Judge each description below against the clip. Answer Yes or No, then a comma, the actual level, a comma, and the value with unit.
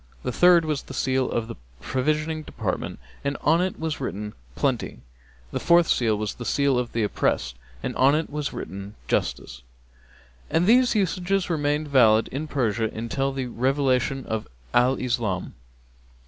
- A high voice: No, low, 135 Hz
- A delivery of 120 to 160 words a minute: Yes, average, 155 wpm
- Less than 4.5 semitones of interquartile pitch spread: No, average, 5.1 semitones